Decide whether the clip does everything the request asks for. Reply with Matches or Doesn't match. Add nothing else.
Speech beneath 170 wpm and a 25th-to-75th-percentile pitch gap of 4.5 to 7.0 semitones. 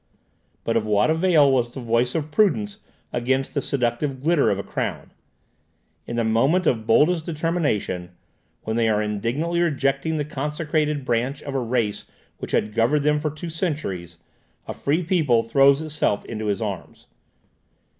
Matches